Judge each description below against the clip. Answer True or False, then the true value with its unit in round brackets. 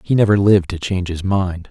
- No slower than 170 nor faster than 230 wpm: False (245 wpm)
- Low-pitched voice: True (95 Hz)